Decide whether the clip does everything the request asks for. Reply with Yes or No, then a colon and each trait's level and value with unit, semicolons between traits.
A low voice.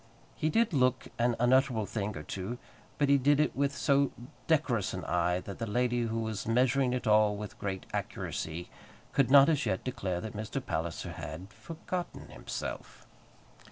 Yes: low, 120 Hz